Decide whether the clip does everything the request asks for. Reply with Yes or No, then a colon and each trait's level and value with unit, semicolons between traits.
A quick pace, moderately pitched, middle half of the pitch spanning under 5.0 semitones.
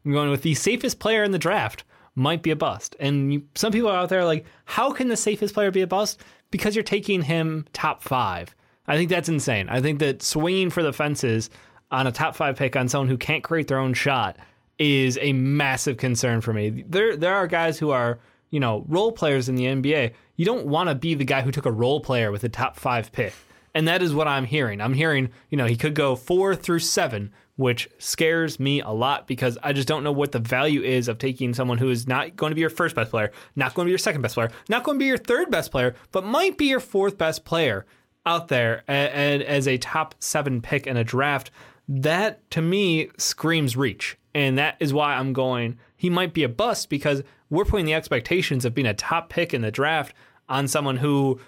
Yes: fast, 240 wpm; medium, 145 Hz; average, 4.4 semitones